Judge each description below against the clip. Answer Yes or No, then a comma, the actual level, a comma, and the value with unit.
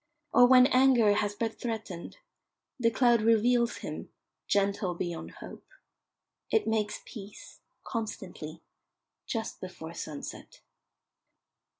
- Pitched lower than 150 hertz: No, high, 220 Hz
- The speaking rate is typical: No, slow, 100 wpm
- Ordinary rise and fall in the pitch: Yes, average, 3.7 semitones